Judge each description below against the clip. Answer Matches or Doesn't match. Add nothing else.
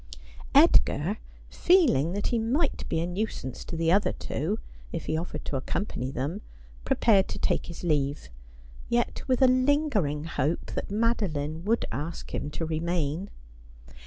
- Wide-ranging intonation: Matches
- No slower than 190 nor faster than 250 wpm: Doesn't match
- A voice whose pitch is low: Doesn't match